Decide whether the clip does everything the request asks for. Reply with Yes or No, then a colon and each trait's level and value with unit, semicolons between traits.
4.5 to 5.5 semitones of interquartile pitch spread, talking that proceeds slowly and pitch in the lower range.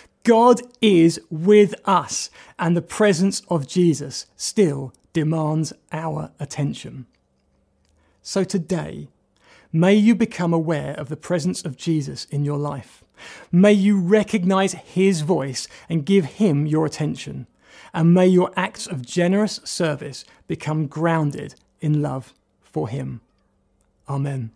No: average, 5.0 semitones; slow, 125 wpm; medium, 165 Hz